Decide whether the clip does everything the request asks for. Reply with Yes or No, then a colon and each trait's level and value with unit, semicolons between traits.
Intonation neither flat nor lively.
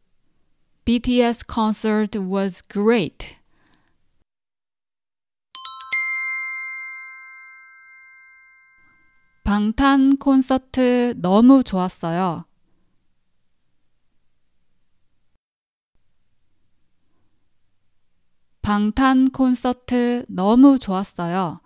No: wide, 7.3 semitones